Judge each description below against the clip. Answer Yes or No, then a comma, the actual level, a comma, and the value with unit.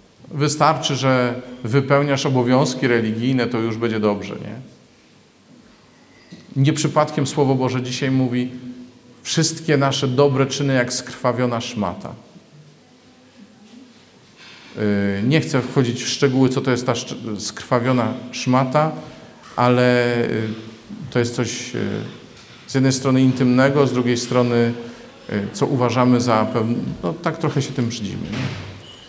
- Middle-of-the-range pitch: No, low, 125 Hz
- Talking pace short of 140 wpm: Yes, average, 115 wpm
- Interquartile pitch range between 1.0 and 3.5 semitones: Yes, narrow, 2.5 semitones